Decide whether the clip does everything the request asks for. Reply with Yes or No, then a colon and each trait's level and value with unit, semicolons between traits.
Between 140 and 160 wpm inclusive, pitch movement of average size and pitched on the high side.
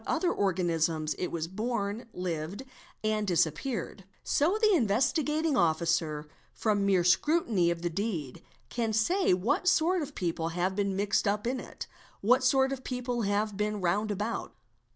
No: average, 150 wpm; wide, 6.2 semitones; high, 205 Hz